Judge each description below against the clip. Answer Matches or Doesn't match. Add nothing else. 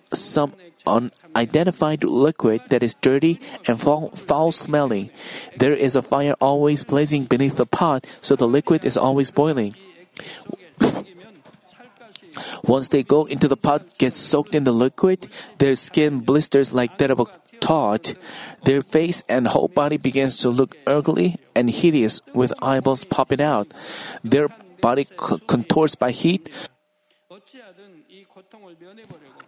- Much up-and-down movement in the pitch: Doesn't match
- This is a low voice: Doesn't match